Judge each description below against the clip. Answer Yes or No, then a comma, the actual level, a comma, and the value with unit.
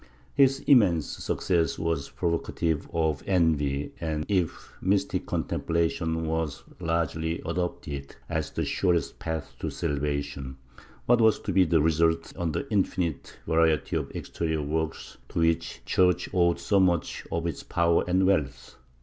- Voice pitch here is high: No, very low, 80 Hz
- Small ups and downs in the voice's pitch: Yes, narrow, 2.2 semitones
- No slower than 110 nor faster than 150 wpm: Yes, average, 145 wpm